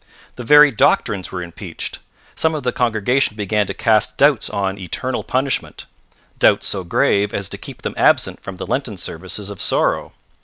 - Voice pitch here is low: Yes, low, 105 Hz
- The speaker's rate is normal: Yes, average, 170 wpm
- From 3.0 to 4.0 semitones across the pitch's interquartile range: No, average, 5.0 semitones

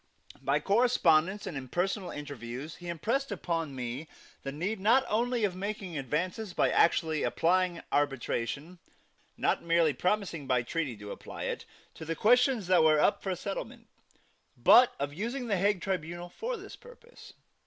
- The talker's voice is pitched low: No, medium, 175 Hz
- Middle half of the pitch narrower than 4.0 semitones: No, wide, 5.6 semitones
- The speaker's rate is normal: Yes, average, 155 wpm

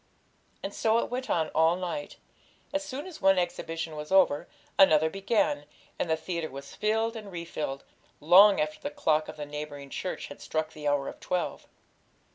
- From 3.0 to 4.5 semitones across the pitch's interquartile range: No, average, 5.1 semitones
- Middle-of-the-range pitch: Yes, medium, 170 Hz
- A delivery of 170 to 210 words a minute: Yes, average, 180 wpm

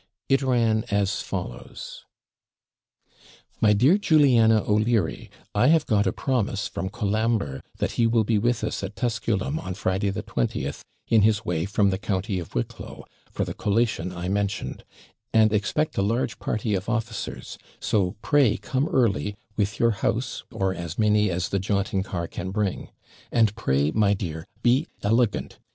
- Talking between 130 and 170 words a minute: Yes, average, 160 wpm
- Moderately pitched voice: No, low, 105 Hz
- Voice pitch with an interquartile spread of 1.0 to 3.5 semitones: Yes, average, 3.2 semitones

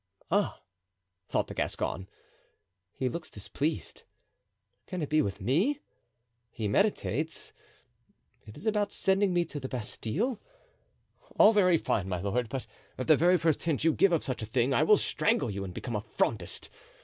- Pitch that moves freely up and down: Yes, wide, 8.3 semitones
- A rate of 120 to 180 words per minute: Yes, average, 160 wpm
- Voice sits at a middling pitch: Yes, medium, 150 Hz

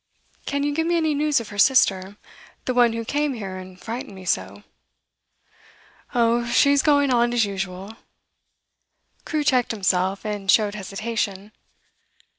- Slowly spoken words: No, average, 145 wpm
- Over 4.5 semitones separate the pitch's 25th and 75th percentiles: Yes, wide, 5.5 semitones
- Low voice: No, high, 225 Hz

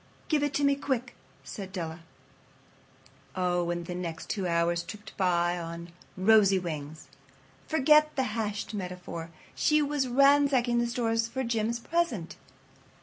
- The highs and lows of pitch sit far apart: Yes, wide, 7.2 semitones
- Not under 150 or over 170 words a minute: No, average, 140 wpm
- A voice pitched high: Yes, high, 210 Hz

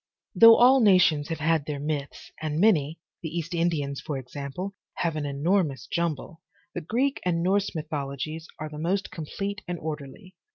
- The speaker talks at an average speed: Yes, average, 165 wpm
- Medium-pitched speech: Yes, medium, 160 Hz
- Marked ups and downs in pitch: No, average, 3.9 semitones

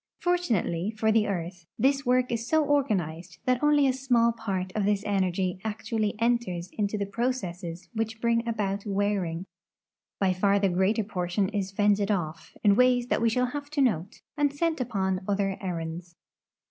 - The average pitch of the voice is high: Yes, high, 205 Hz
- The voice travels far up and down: No, average, 4.4 semitones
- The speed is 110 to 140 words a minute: No, average, 170 wpm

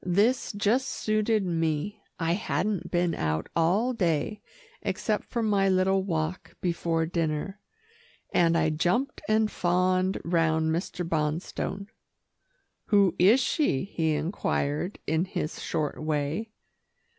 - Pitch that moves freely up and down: No, average, 4.1 semitones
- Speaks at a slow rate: Yes, slow, 120 wpm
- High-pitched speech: No, medium, 175 Hz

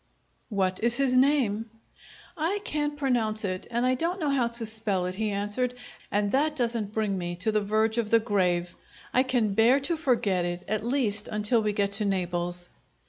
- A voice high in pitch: Yes, high, 220 Hz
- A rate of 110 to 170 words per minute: No, average, 195 wpm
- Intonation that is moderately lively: Yes, average, 4.1 semitones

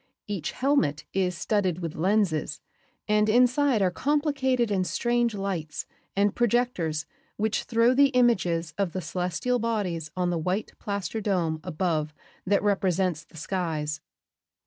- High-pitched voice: Yes, high, 195 Hz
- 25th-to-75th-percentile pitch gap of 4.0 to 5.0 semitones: No, wide, 5.5 semitones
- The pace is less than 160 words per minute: Yes, slow, 135 wpm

